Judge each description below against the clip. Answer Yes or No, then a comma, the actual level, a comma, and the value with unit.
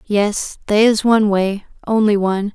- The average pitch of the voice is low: No, high, 205 Hz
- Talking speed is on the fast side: No, average, 140 wpm